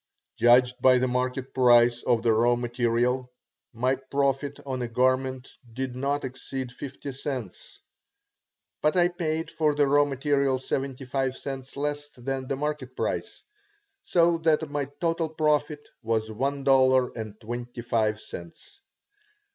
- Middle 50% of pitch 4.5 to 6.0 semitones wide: No, narrow, 2.6 semitones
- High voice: No, low, 130 Hz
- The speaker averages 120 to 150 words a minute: Yes, average, 140 wpm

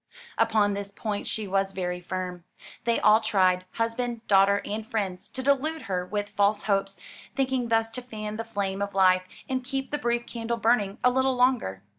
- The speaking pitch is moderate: No, high, 215 Hz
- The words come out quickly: No, average, 185 wpm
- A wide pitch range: No, average, 3.5 semitones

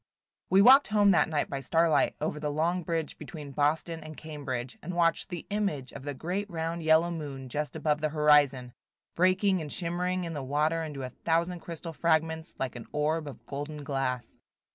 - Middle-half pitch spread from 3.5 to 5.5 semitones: No, average, 2.7 semitones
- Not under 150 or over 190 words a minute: Yes, average, 185 wpm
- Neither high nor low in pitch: Yes, medium, 155 Hz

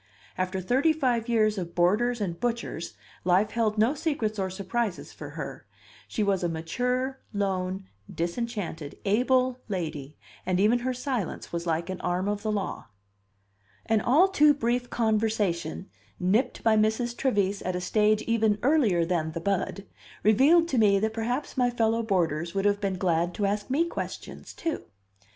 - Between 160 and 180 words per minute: Yes, average, 165 wpm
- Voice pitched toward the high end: Yes, high, 210 Hz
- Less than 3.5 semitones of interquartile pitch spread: No, average, 4.7 semitones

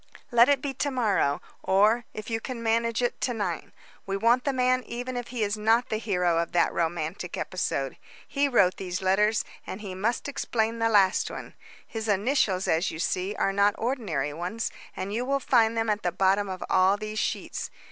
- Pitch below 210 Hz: No, high, 215 Hz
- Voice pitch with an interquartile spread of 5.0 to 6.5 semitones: No, average, 4.0 semitones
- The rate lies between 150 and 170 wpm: No, average, 200 wpm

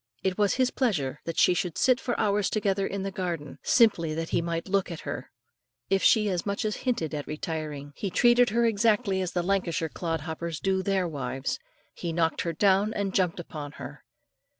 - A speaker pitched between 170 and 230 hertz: Yes, medium, 185 Hz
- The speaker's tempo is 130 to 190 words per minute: No, average, 200 wpm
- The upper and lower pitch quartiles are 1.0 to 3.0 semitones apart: No, average, 3.9 semitones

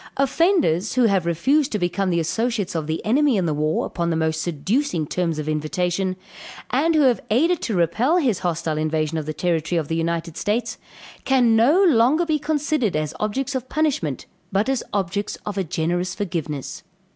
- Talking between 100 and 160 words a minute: No, average, 185 wpm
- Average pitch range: No, wide, 8.0 semitones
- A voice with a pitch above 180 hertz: Yes, high, 190 Hz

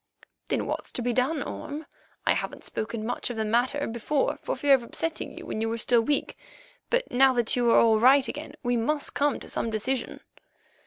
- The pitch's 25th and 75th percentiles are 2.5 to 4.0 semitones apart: Yes, average, 3.6 semitones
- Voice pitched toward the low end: No, high, 245 Hz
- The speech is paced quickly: Yes, fast, 210 wpm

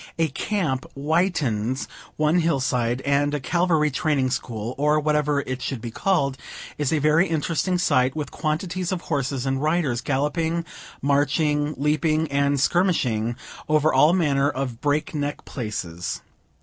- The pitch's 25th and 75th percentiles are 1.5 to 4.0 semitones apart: Yes, average, 3.2 semitones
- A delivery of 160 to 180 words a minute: No, average, 145 wpm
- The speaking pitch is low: No, medium, 145 Hz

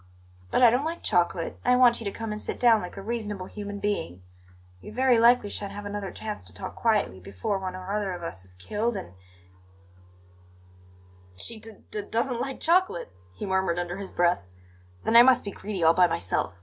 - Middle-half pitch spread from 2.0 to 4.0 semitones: No, average, 5.3 semitones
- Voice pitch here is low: No, high, 200 Hz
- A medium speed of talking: No, fast, 210 wpm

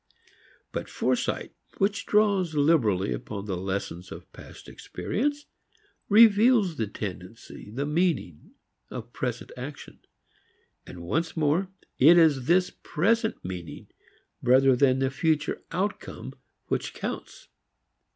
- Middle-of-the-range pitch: Yes, medium, 150 Hz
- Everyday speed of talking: No, slow, 110 wpm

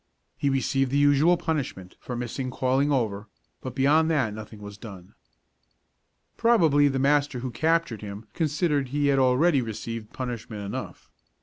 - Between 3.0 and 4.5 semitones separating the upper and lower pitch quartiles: Yes, average, 4.2 semitones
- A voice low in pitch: Yes, low, 130 Hz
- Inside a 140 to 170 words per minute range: Yes, average, 145 wpm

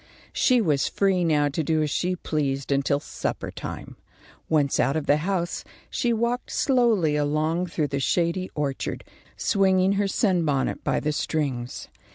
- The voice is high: No, medium, 160 Hz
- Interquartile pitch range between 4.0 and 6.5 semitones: Yes, average, 4.5 semitones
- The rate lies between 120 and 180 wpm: Yes, average, 155 wpm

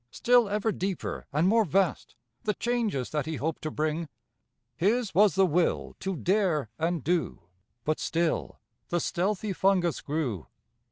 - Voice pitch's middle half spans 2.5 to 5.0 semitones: Yes, average, 4.5 semitones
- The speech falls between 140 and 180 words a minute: Yes, average, 150 wpm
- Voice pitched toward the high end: No, medium, 175 Hz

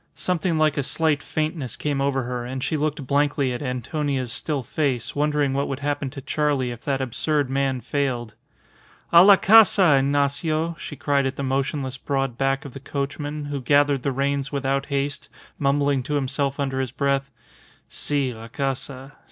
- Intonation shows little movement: Yes, narrow, 1.6 semitones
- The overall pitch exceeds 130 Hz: Yes, medium, 140 Hz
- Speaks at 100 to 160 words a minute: No, average, 175 wpm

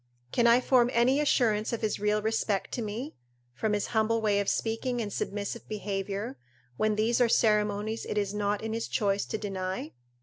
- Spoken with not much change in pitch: Yes, narrow, 2.1 semitones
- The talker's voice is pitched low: No, high, 215 Hz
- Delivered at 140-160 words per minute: No, average, 190 wpm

